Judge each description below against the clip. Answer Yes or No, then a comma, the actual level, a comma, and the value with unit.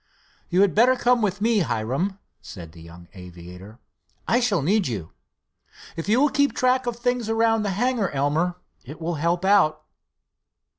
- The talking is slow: No, average, 165 wpm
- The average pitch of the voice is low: No, high, 190 Hz